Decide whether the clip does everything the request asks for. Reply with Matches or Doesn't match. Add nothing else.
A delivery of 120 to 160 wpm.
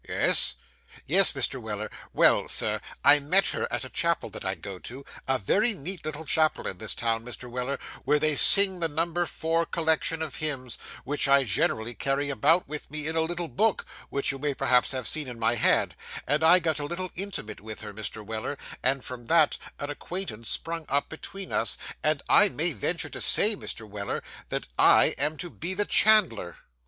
Doesn't match